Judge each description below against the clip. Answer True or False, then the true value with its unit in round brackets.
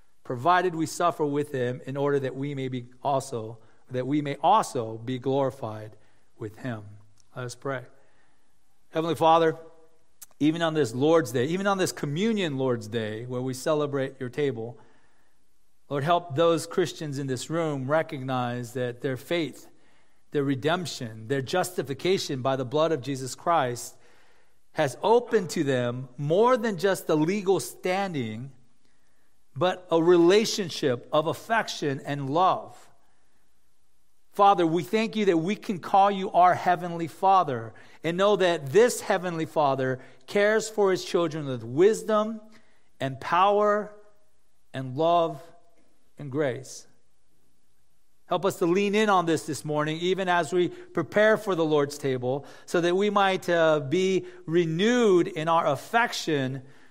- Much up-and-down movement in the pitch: True (5.7 semitones)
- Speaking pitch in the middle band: True (155 Hz)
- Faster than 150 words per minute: False (145 wpm)